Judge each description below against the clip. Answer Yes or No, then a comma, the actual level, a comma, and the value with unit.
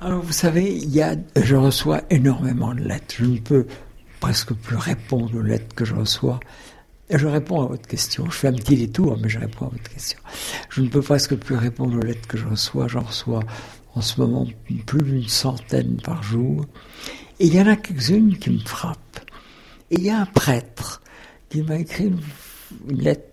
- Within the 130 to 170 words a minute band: No, average, 205 wpm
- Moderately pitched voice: No, low, 130 Hz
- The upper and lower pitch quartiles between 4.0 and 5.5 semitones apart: Yes, average, 4.8 semitones